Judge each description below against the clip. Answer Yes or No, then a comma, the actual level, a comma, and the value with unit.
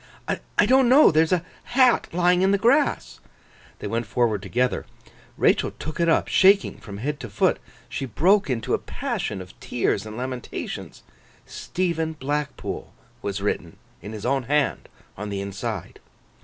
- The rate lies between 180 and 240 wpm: No, average, 160 wpm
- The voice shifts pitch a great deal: Yes, wide, 8.7 semitones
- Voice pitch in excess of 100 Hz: Yes, low, 135 Hz